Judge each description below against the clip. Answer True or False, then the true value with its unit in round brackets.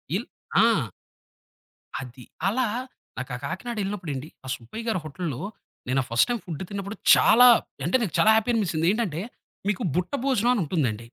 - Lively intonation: True (7.7 semitones)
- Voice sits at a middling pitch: True (180 Hz)